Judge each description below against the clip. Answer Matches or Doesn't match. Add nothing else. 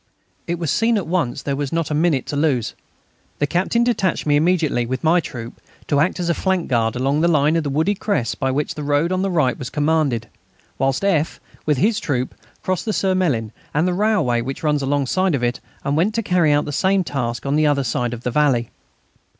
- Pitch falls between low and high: Matches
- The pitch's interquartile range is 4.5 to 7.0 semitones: Matches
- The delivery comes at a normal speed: Doesn't match